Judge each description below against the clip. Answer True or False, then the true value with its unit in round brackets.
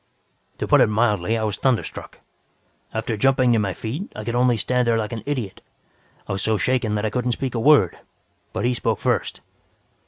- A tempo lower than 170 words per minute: False (205 wpm)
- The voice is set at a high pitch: False (115 Hz)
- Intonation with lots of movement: False (2.8 semitones)